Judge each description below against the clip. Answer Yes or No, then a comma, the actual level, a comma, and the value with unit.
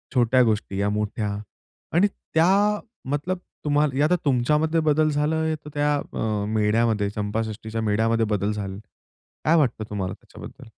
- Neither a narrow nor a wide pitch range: No, wide, 6.1 semitones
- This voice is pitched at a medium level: No, low, 115 Hz